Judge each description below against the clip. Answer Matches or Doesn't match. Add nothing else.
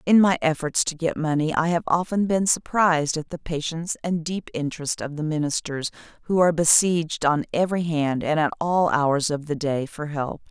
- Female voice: Matches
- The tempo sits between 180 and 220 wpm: Matches